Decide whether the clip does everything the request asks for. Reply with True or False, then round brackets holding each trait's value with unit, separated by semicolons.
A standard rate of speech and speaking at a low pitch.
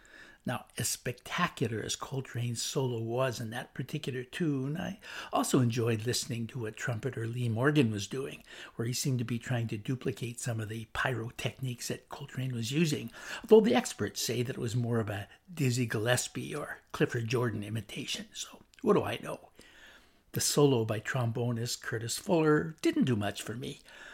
True (175 wpm; 125 Hz)